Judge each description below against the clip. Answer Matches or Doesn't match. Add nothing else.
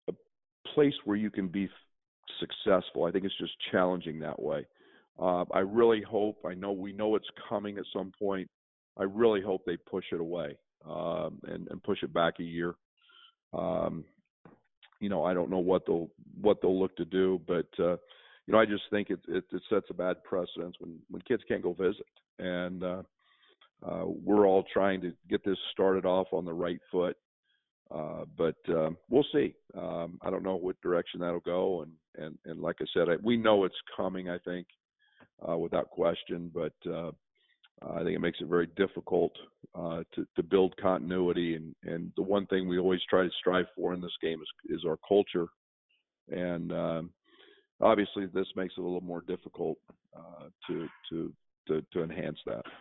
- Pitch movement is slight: Matches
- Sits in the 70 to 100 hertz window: Matches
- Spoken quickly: Doesn't match